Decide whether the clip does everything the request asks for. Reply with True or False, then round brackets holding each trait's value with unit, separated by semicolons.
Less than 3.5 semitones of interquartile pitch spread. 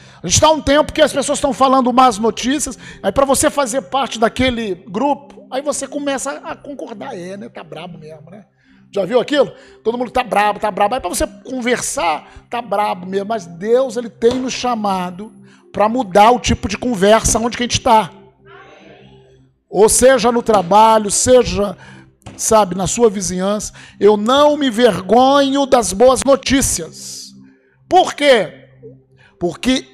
False (5.2 semitones)